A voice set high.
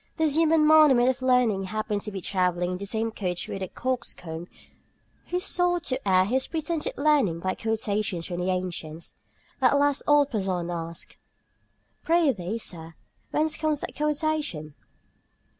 Yes: high, 220 Hz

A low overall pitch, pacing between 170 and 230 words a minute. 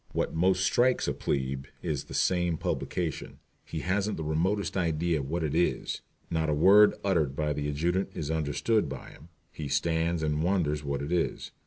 Yes: very low, 80 Hz; average, 185 wpm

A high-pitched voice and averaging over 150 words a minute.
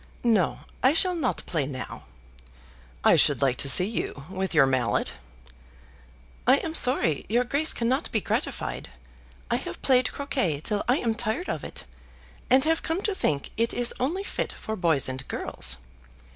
Yes: high, 230 Hz; average, 170 wpm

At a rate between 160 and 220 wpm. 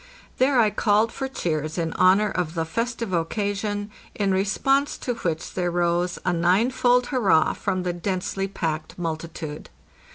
No: average, 150 wpm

